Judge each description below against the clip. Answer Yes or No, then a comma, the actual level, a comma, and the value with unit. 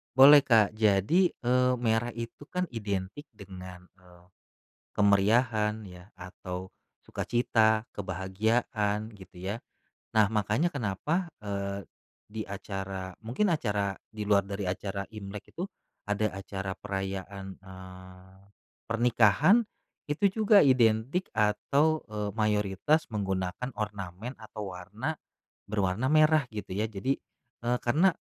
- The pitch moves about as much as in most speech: Yes, average, 4.0 semitones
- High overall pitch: No, low, 105 Hz